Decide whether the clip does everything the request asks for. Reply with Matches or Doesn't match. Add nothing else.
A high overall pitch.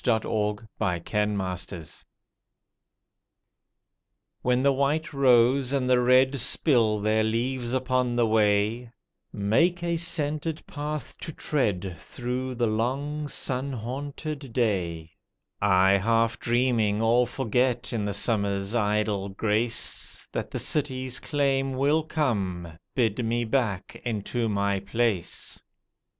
Doesn't match